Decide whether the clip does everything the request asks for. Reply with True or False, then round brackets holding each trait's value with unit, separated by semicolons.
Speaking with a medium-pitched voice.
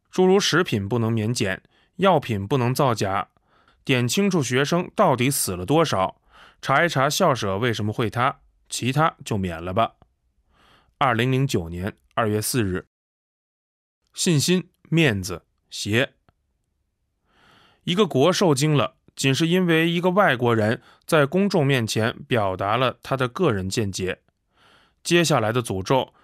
False (130 Hz)